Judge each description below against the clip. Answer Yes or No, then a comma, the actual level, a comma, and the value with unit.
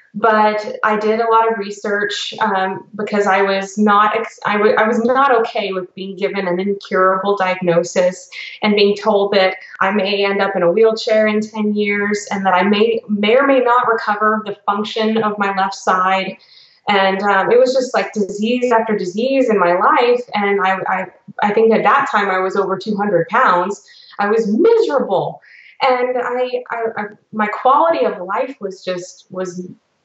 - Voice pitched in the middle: No, high, 210 Hz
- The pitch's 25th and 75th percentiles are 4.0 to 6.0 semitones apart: No, average, 2.7 semitones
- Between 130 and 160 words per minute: No, average, 185 wpm